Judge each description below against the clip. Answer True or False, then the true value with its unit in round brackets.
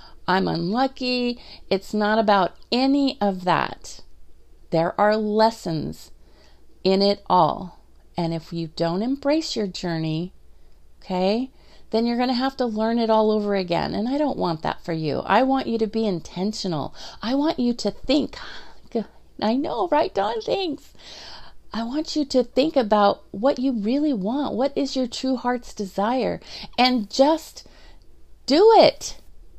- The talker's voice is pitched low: False (220 Hz)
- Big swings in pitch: True (6.2 semitones)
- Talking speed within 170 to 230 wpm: False (155 wpm)